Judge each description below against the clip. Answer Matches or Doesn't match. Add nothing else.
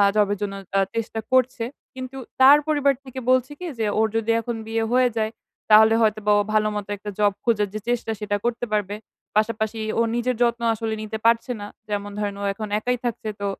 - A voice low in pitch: Doesn't match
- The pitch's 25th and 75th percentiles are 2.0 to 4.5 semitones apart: Matches